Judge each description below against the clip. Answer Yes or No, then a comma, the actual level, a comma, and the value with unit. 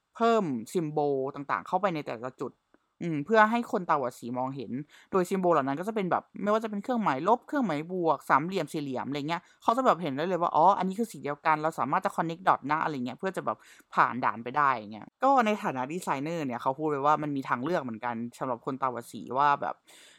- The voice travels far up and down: Yes, wide, 6.8 semitones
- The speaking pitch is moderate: Yes, medium, 155 Hz